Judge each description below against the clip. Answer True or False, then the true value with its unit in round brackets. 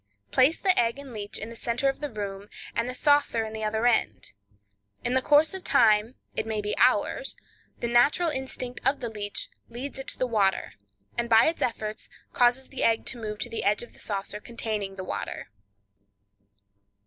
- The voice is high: True (235 Hz)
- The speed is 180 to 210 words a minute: True (190 wpm)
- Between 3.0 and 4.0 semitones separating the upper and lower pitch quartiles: True (3.7 semitones)